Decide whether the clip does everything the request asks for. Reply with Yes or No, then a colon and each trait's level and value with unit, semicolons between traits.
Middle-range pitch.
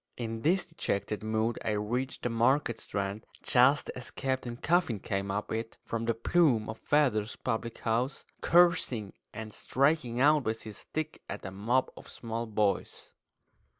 No: low, 115 Hz